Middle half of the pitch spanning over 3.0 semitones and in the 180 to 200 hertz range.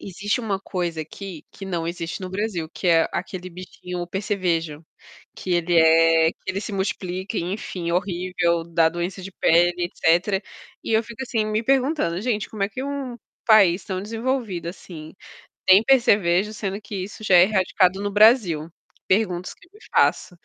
Yes: average, 3.6 semitones; medium, 185 Hz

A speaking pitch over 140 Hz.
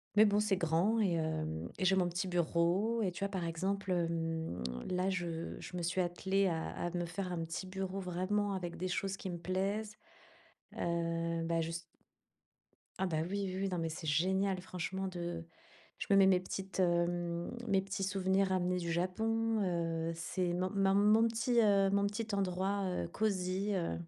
Yes: medium, 185 Hz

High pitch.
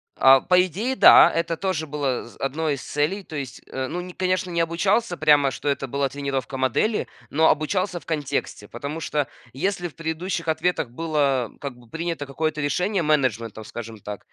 No: medium, 150 Hz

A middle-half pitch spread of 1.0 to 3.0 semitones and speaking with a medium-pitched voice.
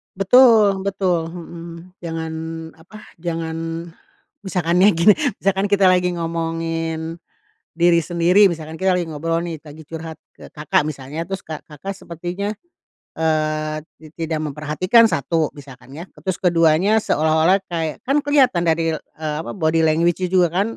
Yes: narrow, 2.6 semitones; medium, 165 Hz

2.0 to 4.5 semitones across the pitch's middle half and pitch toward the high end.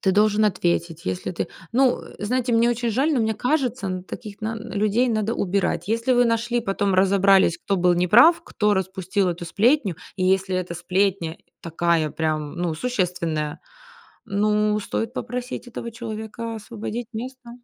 Yes: average, 4.2 semitones; high, 205 Hz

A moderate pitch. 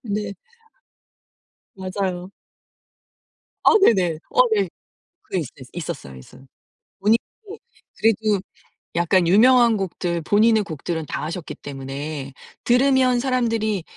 No: high, 195 Hz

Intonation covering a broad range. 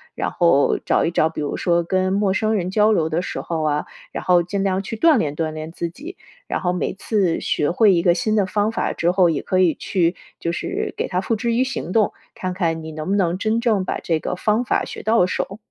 No: average, 4.2 semitones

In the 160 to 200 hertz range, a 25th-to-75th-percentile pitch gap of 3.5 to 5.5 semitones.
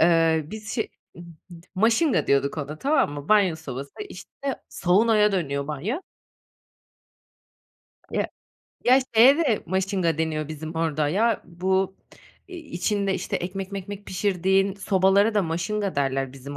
Yes: medium, 185 Hz; average, 4.7 semitones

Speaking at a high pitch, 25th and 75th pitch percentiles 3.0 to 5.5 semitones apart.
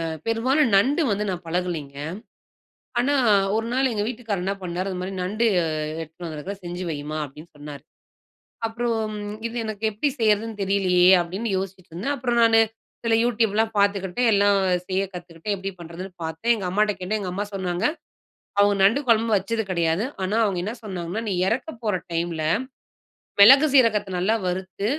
Yes: high, 200 Hz; average, 3.9 semitones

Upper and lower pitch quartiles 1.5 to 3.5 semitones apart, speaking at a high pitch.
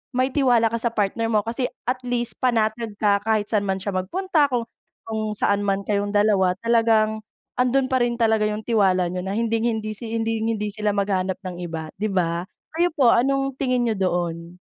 Yes: average, 3.0 semitones; high, 220 Hz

